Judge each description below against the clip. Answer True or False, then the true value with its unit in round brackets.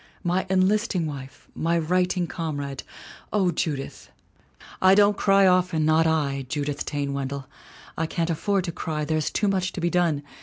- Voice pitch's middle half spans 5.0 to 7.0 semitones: False (3.9 semitones)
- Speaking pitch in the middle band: True (165 Hz)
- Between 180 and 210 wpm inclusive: False (165 wpm)